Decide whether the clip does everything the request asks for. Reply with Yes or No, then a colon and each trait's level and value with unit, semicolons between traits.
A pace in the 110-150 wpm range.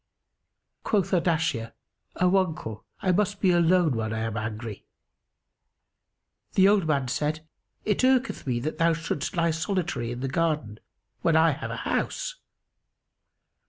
Yes: average, 140 wpm